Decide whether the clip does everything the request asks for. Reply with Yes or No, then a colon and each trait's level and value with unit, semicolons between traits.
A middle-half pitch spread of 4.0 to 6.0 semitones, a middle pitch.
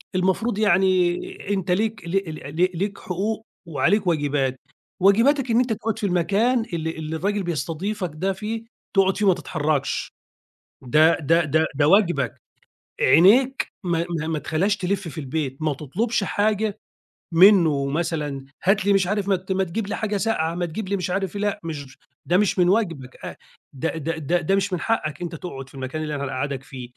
Yes: average, 4.5 semitones; medium, 180 Hz